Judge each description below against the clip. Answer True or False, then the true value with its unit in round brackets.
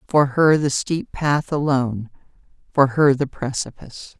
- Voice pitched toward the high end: False (135 Hz)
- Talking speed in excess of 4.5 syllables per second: False (4.4 syllables/s)